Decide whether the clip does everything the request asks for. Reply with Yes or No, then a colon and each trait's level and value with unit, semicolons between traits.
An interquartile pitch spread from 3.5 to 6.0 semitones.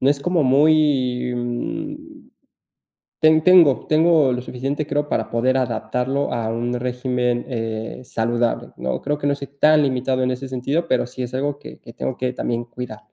No: average, 2.9 semitones